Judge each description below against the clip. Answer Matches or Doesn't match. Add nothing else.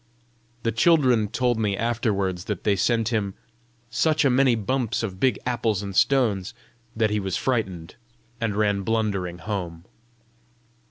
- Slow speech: Doesn't match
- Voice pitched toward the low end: Matches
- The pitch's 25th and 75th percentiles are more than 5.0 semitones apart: Doesn't match